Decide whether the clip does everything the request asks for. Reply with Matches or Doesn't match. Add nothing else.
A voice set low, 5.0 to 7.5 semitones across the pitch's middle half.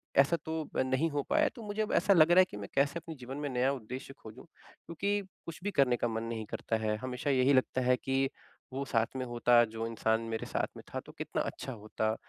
Matches